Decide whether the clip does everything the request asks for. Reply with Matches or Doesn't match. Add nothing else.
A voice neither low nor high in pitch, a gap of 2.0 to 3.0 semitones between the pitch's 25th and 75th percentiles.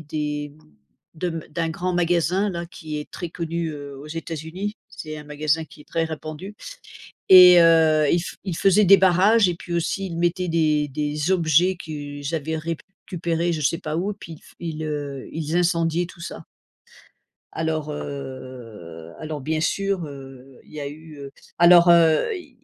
Matches